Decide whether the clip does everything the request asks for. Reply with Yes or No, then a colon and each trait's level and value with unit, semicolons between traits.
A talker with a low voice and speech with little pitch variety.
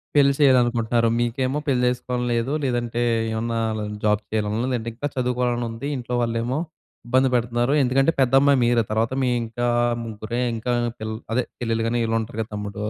Yes: low, 120 Hz; narrow, 1.8 semitones